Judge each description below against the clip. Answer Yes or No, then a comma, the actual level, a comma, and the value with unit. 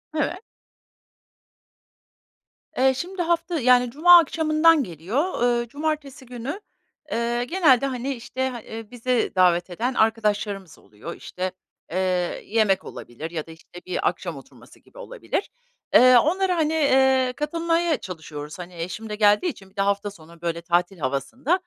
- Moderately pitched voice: No, high, 240 Hz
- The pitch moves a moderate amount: No, wide, 8.6 semitones